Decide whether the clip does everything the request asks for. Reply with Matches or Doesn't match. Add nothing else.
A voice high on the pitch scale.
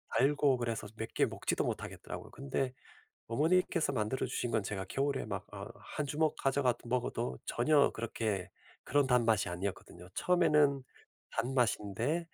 Doesn't match